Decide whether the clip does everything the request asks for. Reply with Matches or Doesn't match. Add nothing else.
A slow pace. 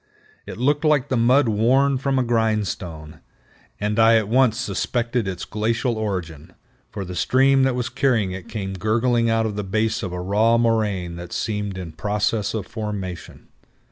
Doesn't match